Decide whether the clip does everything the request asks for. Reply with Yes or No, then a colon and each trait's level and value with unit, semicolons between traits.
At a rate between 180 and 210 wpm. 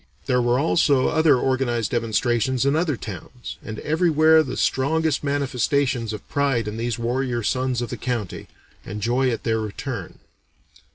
No: average, 155 wpm